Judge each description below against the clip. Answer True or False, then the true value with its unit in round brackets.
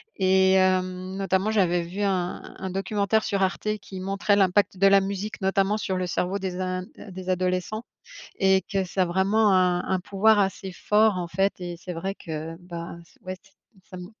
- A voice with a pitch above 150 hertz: True (190 Hz)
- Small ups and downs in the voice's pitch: True (1.4 semitones)